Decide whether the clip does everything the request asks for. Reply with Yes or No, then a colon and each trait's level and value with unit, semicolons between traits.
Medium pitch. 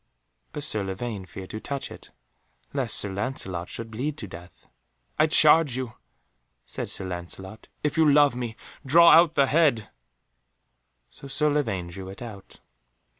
No: low, 120 Hz